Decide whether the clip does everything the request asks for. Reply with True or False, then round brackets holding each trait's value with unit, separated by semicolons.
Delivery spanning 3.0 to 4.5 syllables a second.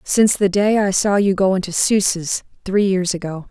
False (5.0 syllables/s)